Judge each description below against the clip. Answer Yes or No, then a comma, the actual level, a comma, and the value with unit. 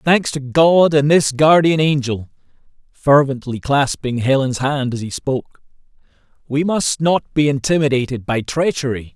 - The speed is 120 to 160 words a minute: Yes, average, 140 wpm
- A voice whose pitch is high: No, medium, 140 Hz